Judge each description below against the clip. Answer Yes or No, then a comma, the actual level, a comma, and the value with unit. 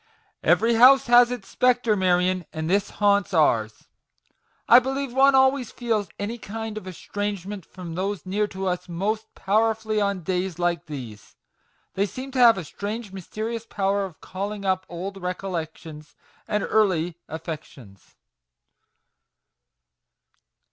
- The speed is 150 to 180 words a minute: No, slow, 135 wpm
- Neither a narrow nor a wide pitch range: Yes, average, 3.8 semitones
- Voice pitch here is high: Yes, high, 200 Hz